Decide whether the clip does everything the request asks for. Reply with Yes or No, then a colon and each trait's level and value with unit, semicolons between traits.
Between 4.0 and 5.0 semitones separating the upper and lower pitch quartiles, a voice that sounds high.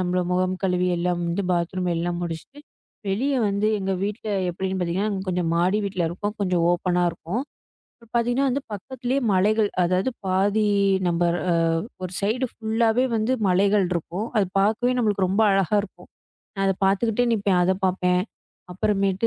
No: average, 3.1 semitones; high, 195 Hz